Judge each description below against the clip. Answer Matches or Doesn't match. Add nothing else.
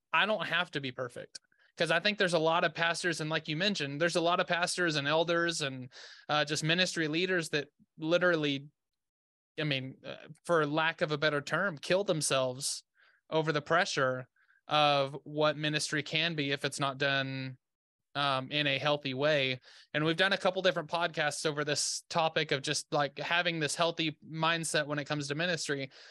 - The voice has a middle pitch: Matches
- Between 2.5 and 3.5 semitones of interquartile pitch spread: Matches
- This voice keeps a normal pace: Matches